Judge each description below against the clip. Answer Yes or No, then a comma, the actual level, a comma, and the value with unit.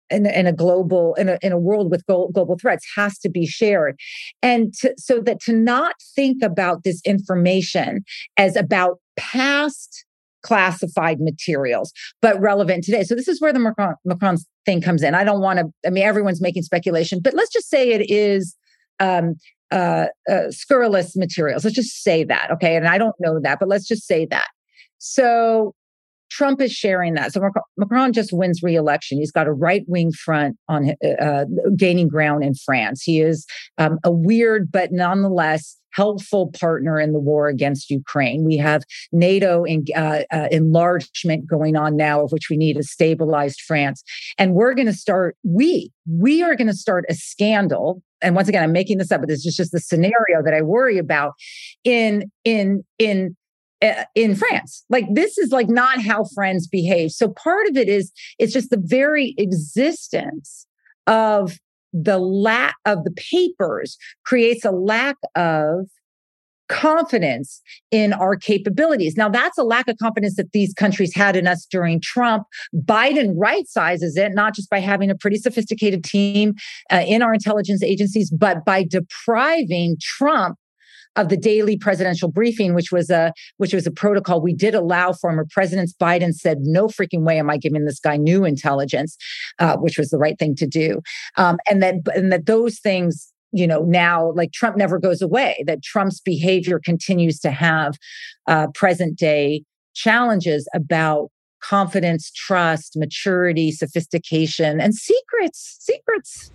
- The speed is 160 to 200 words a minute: Yes, average, 170 wpm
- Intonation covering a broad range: No, average, 4.7 semitones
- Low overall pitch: No, medium, 185 Hz